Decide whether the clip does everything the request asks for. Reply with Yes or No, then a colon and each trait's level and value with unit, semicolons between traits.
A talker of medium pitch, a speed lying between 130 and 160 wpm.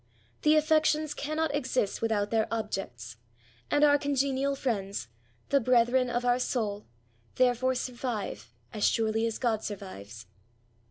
No: high, 240 Hz; average, 140 wpm